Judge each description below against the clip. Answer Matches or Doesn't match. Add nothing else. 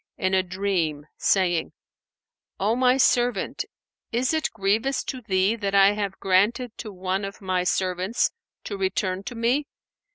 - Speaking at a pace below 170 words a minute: Matches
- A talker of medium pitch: Doesn't match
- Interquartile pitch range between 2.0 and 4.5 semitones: Matches